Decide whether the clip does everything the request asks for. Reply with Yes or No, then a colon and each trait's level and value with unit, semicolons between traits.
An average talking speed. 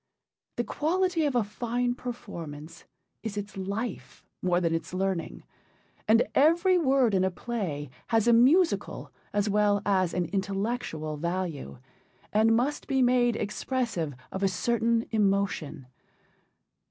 No: slow, 130 wpm